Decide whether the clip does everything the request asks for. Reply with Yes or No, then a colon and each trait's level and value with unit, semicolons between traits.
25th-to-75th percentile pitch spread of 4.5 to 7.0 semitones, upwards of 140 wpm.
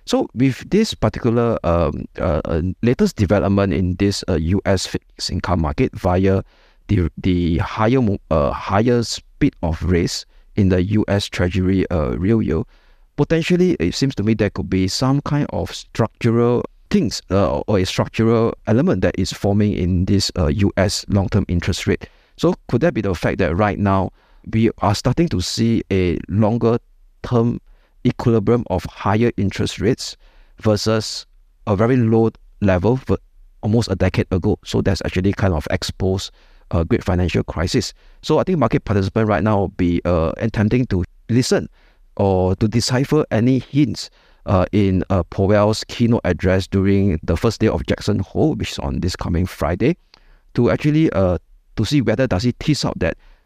No: average, 3.9 semitones; average, 170 wpm